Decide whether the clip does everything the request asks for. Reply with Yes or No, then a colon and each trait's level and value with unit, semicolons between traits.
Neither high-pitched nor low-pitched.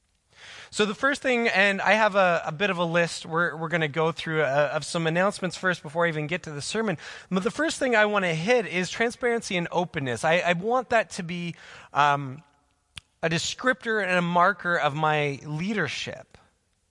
Yes: medium, 175 Hz